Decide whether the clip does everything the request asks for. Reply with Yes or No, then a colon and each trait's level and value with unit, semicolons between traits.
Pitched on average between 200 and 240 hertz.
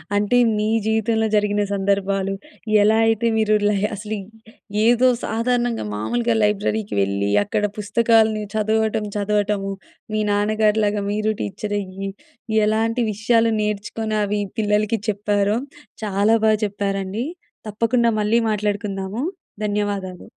Yes: high, 210 Hz